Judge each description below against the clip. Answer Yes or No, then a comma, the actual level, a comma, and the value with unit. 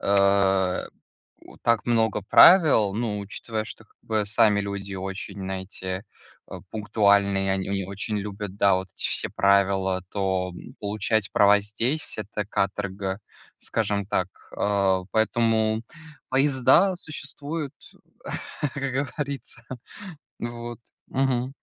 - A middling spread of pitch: Yes, average, 3.0 semitones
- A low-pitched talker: Yes, low, 105 Hz